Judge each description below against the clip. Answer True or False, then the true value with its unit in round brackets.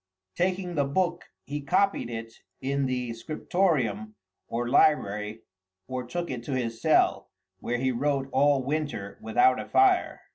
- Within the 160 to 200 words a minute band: False (145 wpm)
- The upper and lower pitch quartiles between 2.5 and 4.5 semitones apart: False (4.9 semitones)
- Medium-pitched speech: False (130 Hz)